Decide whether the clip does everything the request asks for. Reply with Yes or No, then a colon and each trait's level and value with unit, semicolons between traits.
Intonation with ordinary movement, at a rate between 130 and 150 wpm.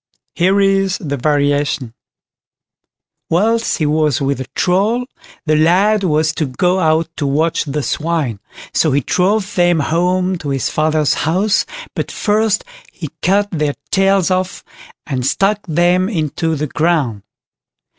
Yes: average, 4.2 semitones; average, 140 wpm